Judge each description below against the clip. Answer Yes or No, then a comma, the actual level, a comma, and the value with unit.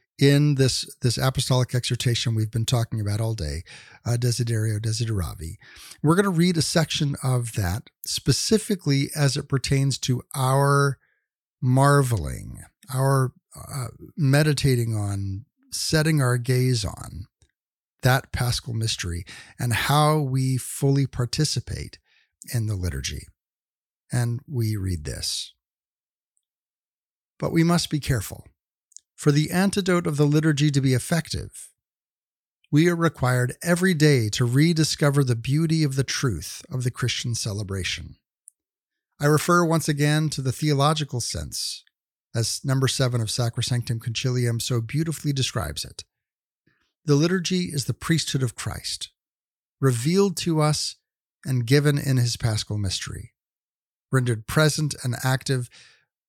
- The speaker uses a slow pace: Yes, slow, 130 wpm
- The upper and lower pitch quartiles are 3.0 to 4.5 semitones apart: Yes, average, 4.2 semitones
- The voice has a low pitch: Yes, low, 130 Hz